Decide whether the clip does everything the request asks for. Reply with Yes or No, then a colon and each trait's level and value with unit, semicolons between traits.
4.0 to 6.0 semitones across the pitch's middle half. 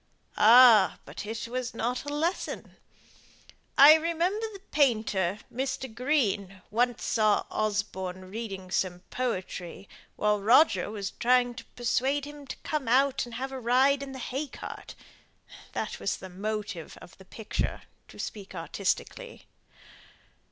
Yes: average, 5.0 semitones